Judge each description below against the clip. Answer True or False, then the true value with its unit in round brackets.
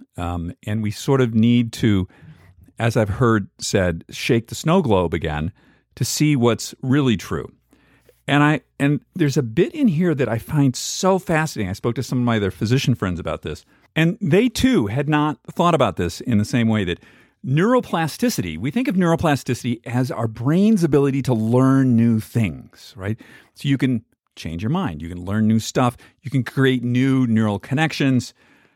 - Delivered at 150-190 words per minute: True (185 wpm)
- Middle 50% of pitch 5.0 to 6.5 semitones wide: True (5.3 semitones)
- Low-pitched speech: True (125 Hz)